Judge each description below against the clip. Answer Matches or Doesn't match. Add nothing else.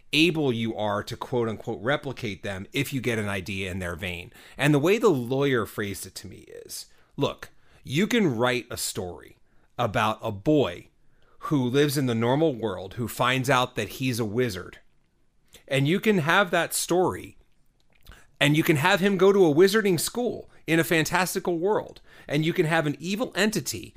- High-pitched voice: Doesn't match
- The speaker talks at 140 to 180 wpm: Doesn't match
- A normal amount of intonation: Doesn't match